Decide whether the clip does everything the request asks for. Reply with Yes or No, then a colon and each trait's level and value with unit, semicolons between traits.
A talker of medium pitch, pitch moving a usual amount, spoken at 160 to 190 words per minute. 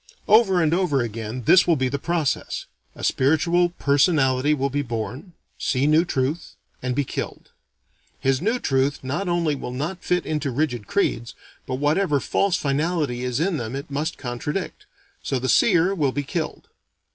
Yes: medium, 145 Hz; average, 4.9 semitones; average, 170 wpm